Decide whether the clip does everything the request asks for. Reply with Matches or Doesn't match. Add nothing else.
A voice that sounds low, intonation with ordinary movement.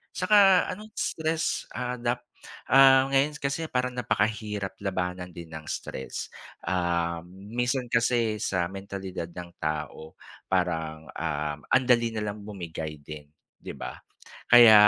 Doesn't match